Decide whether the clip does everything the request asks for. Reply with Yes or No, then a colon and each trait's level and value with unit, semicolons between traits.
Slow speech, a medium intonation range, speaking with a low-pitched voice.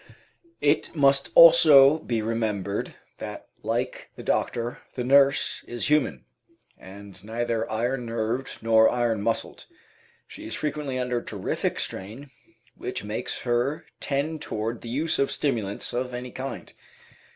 Yes: slow, 130 wpm; average, 3.7 semitones; low, 120 Hz